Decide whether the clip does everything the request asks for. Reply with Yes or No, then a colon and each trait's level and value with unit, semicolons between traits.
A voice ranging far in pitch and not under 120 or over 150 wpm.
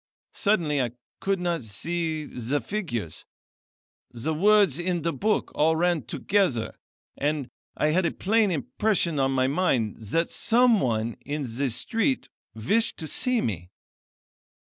Yes: wide, 7.0 semitones; average, 140 wpm